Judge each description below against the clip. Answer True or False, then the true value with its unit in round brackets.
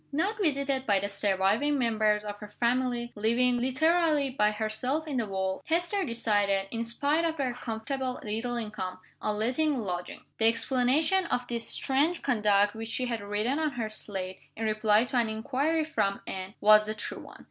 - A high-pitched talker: True (235 Hz)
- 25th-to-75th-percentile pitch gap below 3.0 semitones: False (4.6 semitones)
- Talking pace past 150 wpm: True (180 wpm)